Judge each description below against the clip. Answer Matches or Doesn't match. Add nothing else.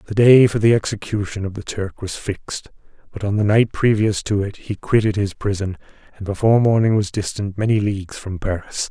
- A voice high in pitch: Doesn't match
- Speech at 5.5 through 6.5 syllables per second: Matches